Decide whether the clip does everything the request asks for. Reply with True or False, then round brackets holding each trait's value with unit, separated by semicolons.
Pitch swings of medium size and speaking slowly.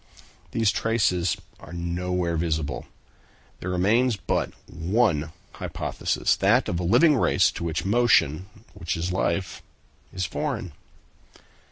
True (4.1 semitones; 120 wpm)